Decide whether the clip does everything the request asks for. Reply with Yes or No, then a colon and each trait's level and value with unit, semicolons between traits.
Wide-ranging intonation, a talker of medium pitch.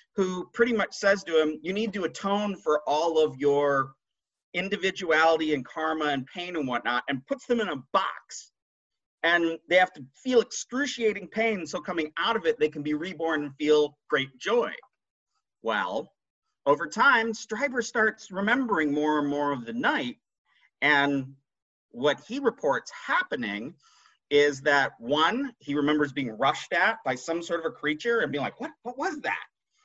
Yes: wide, 7.4 semitones; medium, 170 Hz